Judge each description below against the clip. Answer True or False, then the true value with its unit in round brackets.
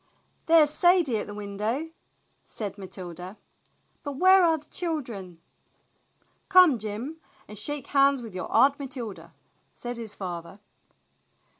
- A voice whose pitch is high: True (235 Hz)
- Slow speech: True (125 wpm)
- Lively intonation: True (6.8 semitones)